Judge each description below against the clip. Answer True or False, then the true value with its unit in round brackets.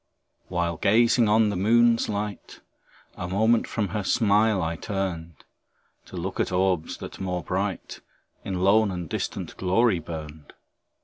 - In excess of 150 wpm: False (140 wpm)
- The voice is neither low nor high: False (95 Hz)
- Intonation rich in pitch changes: False (3.4 semitones)